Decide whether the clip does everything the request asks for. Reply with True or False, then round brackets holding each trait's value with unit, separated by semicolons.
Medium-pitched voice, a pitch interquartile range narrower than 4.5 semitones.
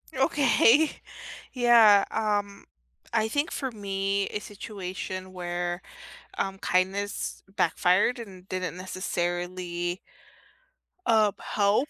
False (195 Hz; 3.2 semitones)